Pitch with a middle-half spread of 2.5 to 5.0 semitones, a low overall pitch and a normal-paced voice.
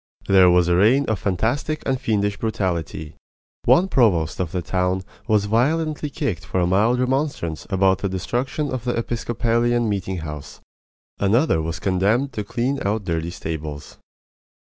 No: wide, 5.4 semitones; low, 100 Hz; average, 150 wpm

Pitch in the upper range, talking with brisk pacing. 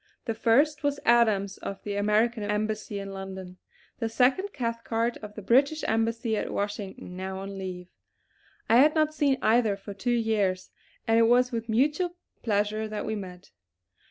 No: high, 220 Hz; average, 165 wpm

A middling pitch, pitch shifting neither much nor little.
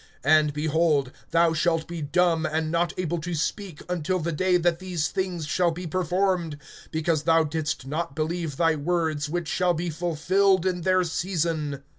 No: medium, 165 Hz; narrow, 2.3 semitones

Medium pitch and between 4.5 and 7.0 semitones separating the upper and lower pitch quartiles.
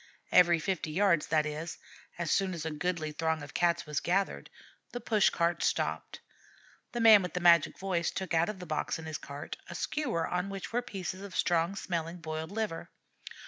No: medium, 175 Hz; average, 3.3 semitones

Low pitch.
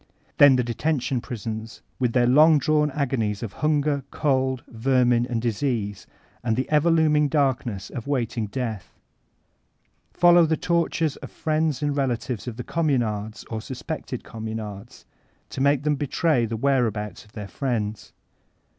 Yes: low, 130 Hz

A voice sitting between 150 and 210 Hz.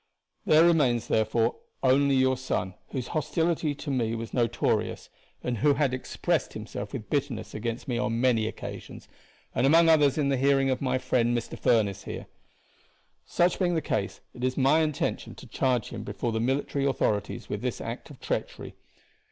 No: low, 130 Hz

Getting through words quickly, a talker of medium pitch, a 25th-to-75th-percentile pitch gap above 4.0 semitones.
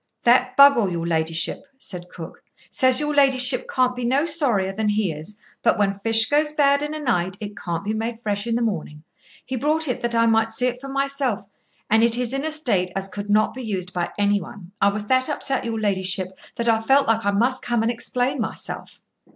No: fast, 225 wpm; high, 225 Hz; average, 4.4 semitones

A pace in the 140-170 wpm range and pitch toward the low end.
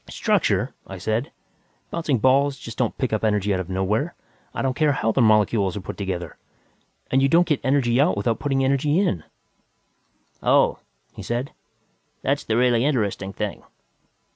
Yes: average, 165 wpm; low, 120 Hz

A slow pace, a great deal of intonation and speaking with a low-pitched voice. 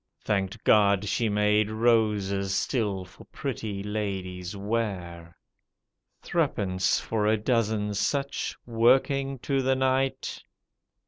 No: slow, 105 wpm; average, 3.1 semitones; low, 105 Hz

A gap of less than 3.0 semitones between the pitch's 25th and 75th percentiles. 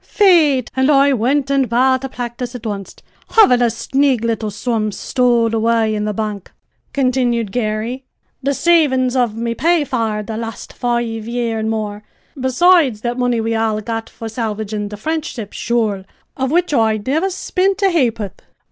No: average, 3.4 semitones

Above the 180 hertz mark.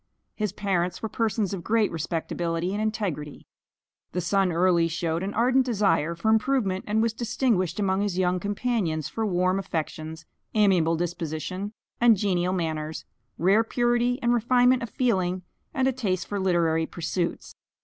Yes: high, 190 Hz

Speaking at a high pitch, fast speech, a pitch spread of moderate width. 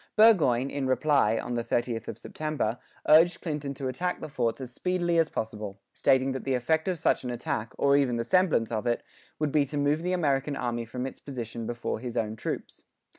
No: low, 130 Hz; fast, 210 wpm; average, 4.5 semitones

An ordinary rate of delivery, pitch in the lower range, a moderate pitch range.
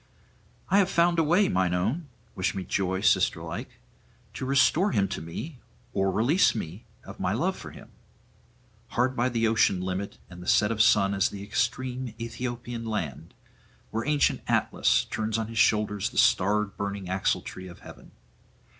Yes: average, 165 wpm; low, 110 Hz; average, 4.7 semitones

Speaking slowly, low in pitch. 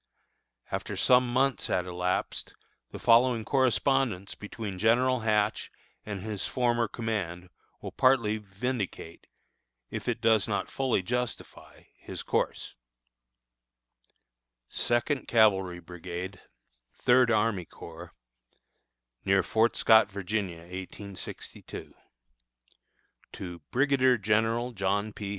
Yes: slow, 100 wpm; low, 110 Hz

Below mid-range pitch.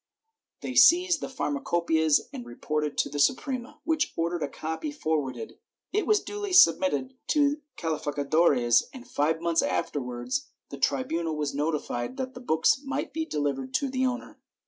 No: medium, 170 Hz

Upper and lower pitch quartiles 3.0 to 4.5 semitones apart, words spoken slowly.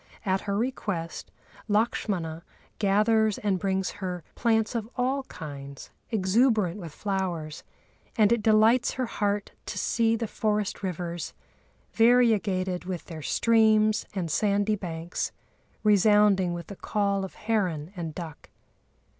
Yes: average, 3.6 semitones; slow, 125 wpm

